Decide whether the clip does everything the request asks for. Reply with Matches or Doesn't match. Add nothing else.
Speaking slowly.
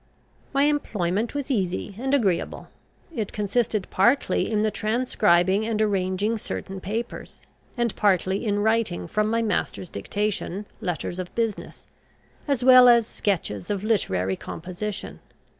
Matches